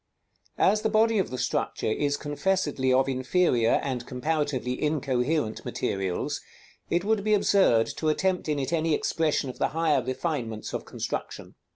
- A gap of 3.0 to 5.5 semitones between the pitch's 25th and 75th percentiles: Yes, average, 5.2 semitones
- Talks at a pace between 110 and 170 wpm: Yes, average, 160 wpm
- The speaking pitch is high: No, medium, 145 Hz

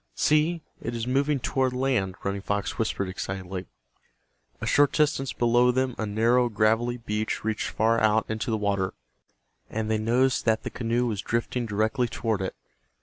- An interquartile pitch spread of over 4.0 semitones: No, average, 2.8 semitones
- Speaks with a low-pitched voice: Yes, low, 115 Hz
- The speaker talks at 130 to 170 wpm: Yes, average, 165 wpm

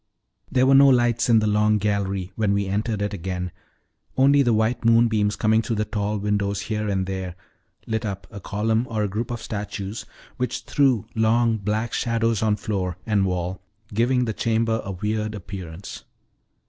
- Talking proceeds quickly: No, average, 175 wpm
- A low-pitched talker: Yes, low, 105 Hz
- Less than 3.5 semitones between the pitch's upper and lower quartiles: Yes, narrow, 2.4 semitones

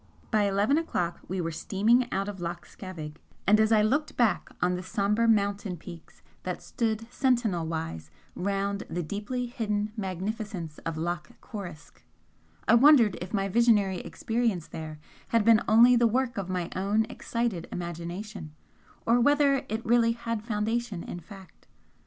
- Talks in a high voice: Yes, high, 205 Hz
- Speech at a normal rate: Yes, average, 155 wpm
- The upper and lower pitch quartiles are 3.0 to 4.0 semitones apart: No, average, 4.4 semitones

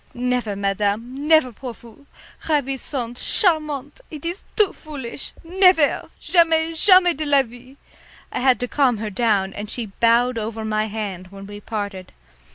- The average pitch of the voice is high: Yes, high, 245 Hz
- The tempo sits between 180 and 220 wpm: No, average, 155 wpm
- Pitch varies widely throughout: Yes, wide, 6.0 semitones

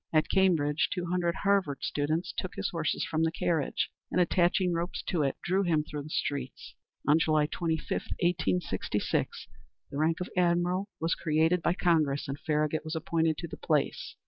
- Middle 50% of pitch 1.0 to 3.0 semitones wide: Yes, narrow, 2.6 semitones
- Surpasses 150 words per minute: Yes, average, 170 wpm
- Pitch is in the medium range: Yes, medium, 165 Hz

